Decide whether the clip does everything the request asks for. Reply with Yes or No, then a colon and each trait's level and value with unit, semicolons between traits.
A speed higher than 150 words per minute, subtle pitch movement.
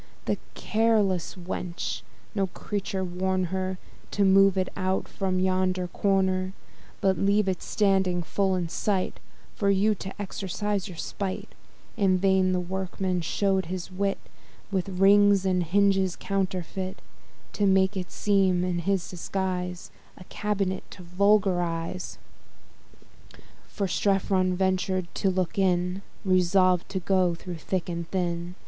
No: slow, 135 wpm; narrow, 1.4 semitones